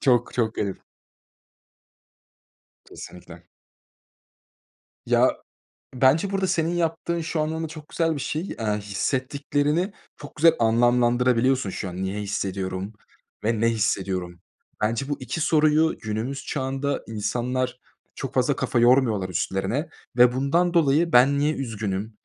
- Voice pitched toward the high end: No, low, 130 Hz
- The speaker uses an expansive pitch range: Yes, wide, 5.7 semitones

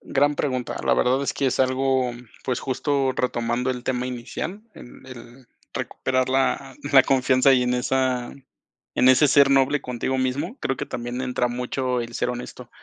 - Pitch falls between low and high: No, low, 130 Hz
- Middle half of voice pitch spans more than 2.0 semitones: No, narrow, 1.3 semitones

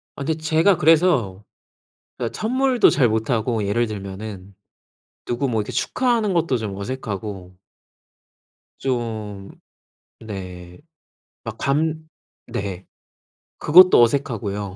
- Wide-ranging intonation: Yes, wide, 7.8 semitones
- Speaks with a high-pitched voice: No, low, 115 Hz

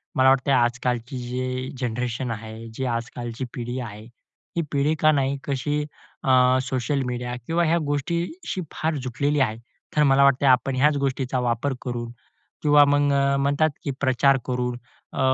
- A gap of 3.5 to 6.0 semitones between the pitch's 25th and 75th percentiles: No, narrow, 2.5 semitones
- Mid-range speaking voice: No, low, 130 Hz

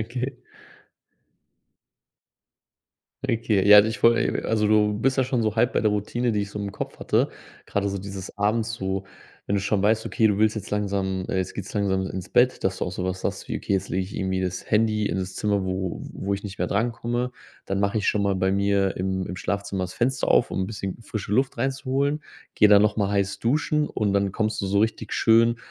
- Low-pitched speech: Yes, low, 105 Hz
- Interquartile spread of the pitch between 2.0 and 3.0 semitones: Yes, average, 2.7 semitones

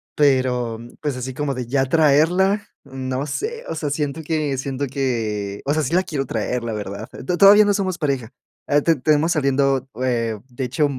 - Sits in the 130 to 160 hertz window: Yes, medium, 140 Hz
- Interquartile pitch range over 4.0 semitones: No, average, 3.7 semitones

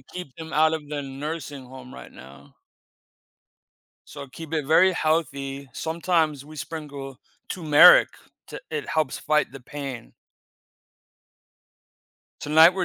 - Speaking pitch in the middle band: Yes, medium, 150 Hz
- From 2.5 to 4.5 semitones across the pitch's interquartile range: Yes, average, 2.9 semitones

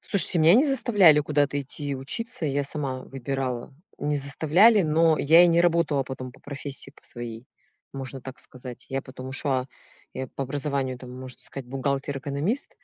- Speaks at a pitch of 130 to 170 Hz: Yes, medium, 140 Hz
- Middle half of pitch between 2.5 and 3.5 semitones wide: Yes, average, 3.2 semitones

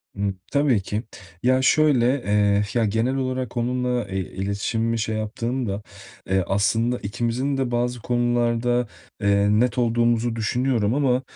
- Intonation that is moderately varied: Yes, average, 3.0 semitones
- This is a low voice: Yes, low, 120 Hz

